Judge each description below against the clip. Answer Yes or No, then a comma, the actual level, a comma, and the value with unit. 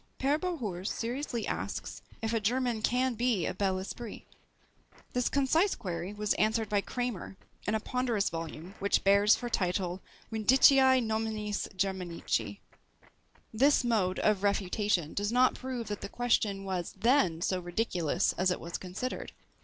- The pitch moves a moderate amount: Yes, average, 4.5 semitones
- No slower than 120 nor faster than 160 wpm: Yes, average, 145 wpm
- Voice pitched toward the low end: No, high, 210 Hz